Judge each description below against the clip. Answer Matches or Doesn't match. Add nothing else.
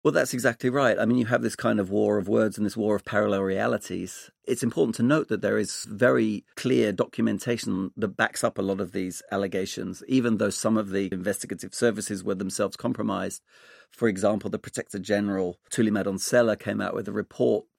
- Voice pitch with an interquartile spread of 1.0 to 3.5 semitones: Matches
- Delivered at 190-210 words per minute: Matches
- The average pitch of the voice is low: Matches